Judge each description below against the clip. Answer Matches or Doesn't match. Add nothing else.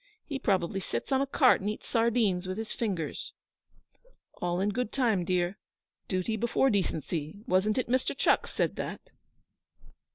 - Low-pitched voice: Doesn't match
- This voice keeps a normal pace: Matches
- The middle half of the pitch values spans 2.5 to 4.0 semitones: Doesn't match